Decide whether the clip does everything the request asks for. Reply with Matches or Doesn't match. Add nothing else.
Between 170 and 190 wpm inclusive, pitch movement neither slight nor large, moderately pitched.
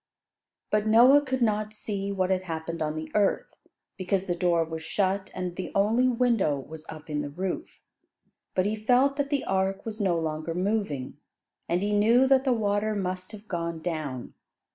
Doesn't match